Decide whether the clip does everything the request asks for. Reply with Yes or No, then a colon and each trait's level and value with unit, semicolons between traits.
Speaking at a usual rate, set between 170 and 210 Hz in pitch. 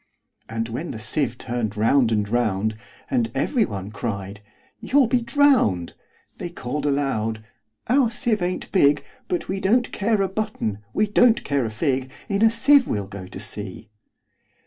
No: average, 155 wpm; medium, 140 Hz